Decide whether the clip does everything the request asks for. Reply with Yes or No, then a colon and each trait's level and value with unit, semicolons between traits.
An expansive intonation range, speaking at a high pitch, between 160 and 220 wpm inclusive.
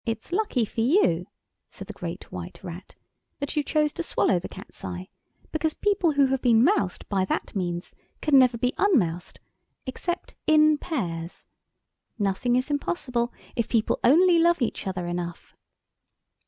Yes: wide, 8.4 semitones; very high, 250 Hz; average, 165 wpm